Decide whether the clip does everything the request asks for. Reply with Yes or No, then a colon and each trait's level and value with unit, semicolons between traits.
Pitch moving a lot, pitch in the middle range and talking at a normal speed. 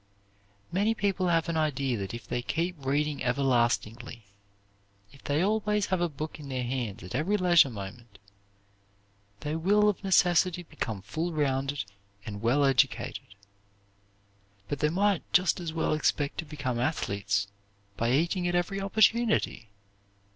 Yes: wide, 6.3 semitones; medium, 150 Hz; average, 145 wpm